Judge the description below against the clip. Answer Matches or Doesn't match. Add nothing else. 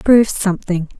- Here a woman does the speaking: Matches